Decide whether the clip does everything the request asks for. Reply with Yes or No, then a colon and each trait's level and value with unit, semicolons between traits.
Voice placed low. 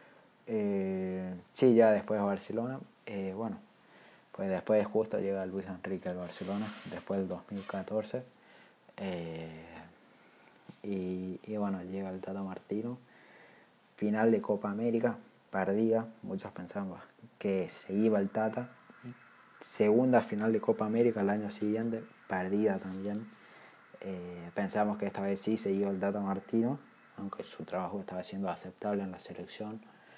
Yes: low, 100 Hz